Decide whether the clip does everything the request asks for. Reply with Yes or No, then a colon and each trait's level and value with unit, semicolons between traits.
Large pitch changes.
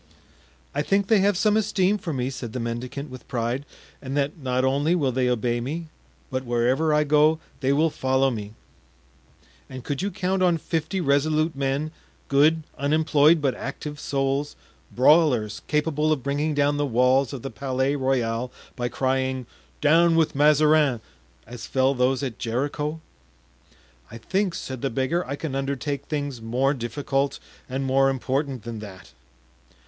No: average, 3.0 semitones